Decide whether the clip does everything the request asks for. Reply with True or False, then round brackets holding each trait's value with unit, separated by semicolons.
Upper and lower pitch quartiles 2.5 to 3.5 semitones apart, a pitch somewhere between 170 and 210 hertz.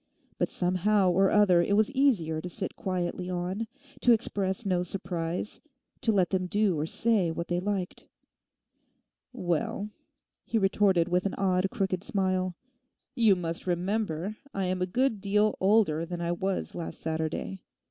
True (2.8 semitones; 185 Hz)